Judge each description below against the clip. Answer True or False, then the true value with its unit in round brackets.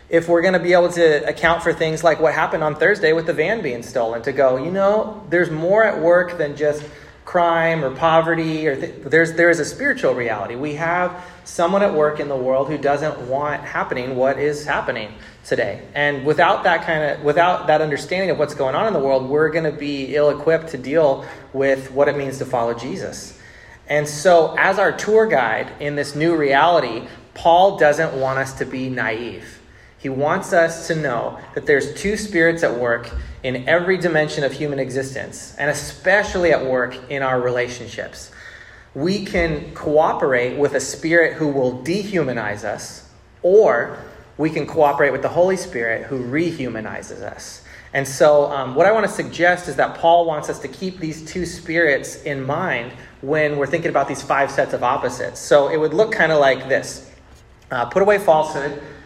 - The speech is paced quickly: False (190 wpm)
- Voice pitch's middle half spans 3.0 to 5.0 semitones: True (3.9 semitones)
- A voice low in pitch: False (150 Hz)